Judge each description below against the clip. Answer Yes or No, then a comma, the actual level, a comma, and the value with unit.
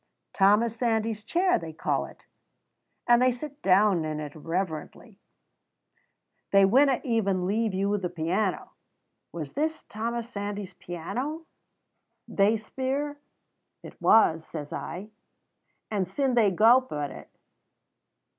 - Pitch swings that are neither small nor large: Yes, average, 5.0 semitones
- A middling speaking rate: No, slow, 120 wpm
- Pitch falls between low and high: No, high, 210 Hz